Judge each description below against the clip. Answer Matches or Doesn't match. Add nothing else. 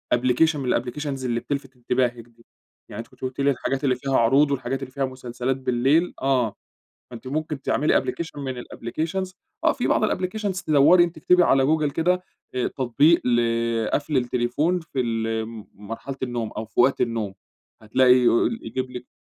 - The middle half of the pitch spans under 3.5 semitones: Doesn't match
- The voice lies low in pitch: Matches